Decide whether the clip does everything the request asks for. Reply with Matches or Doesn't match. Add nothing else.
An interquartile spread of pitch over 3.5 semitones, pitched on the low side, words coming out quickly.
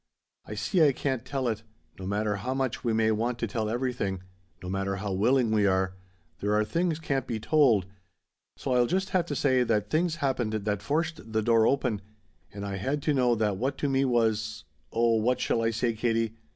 Matches